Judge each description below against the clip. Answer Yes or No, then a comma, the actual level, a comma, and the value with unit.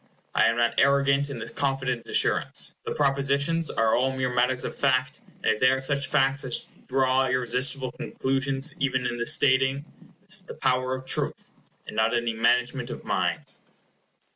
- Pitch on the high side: No, low, 130 Hz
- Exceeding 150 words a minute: Yes, average, 175 wpm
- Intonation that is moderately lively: No, narrow, 1.8 semitones